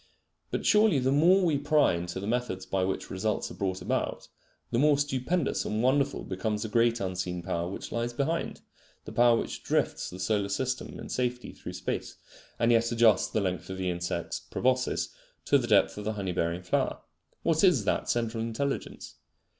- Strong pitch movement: Yes, wide, 5.8 semitones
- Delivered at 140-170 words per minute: No, average, 185 wpm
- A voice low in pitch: Yes, low, 115 Hz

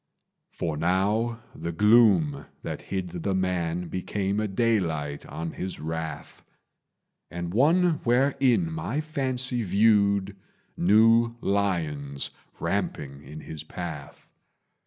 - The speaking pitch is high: No, very low, 95 Hz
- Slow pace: Yes, slow, 105 wpm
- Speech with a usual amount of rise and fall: No, wide, 6.0 semitones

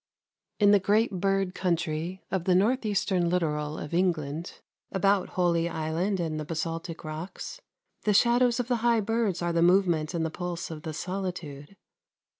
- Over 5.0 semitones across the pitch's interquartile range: No, average, 3.4 semitones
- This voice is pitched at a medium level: Yes, medium, 180 Hz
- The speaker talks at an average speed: Yes, average, 165 wpm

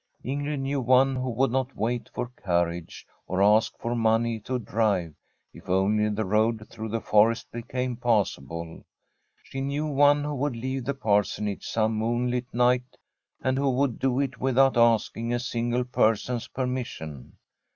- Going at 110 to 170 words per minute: Yes, average, 160 wpm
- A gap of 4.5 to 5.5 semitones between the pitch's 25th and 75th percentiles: No, average, 3.2 semitones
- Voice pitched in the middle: No, low, 120 Hz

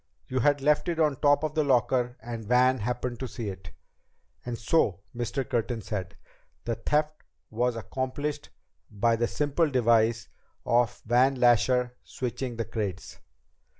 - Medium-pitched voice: No, low, 125 Hz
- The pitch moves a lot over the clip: No, average, 2.9 semitones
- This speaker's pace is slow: No, average, 150 wpm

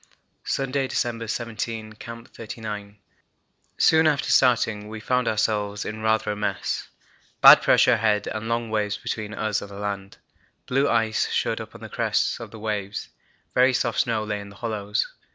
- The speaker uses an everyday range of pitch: No, narrow, 2.0 semitones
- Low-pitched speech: Yes, low, 110 Hz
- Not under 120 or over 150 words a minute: No, average, 165 wpm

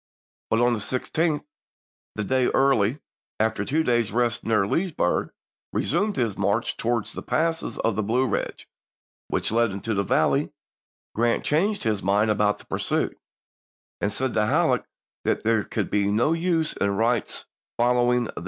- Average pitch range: Yes, average, 3.9 semitones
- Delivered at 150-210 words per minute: Yes, average, 160 wpm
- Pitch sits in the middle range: No, low, 115 Hz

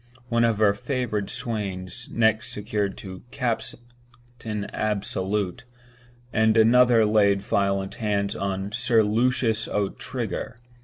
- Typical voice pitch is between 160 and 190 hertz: No, low, 110 Hz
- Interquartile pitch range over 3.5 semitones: No, average, 2.7 semitones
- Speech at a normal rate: No, slow, 100 wpm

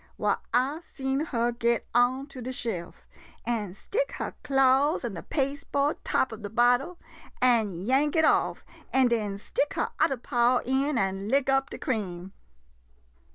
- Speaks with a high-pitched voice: Yes, very high, 250 Hz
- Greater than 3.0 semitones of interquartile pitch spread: Yes, average, 3.5 semitones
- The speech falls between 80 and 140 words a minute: No, average, 160 wpm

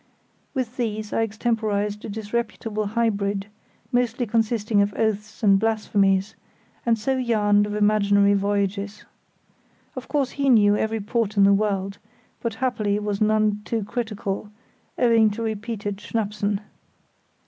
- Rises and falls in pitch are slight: Yes, narrow, 1.9 semitones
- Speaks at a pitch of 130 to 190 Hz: No, high, 210 Hz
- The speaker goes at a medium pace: No, slow, 130 wpm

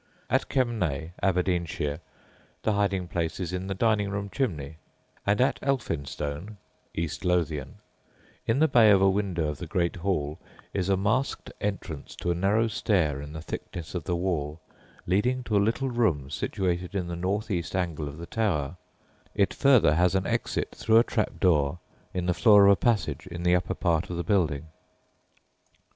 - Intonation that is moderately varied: Yes, average, 3.7 semitones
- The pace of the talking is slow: No, average, 175 wpm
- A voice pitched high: No, very low, 90 Hz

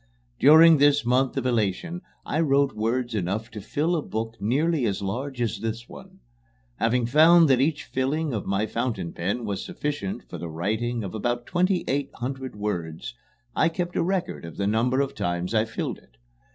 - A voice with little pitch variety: No, wide, 5.4 semitones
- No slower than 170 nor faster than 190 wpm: Yes, average, 185 wpm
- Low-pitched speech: Yes, low, 120 Hz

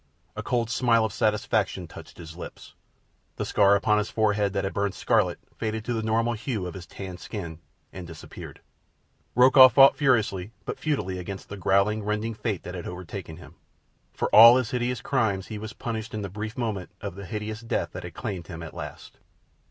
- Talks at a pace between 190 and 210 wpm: Yes, average, 195 wpm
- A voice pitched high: No, low, 105 Hz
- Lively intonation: No, average, 3.2 semitones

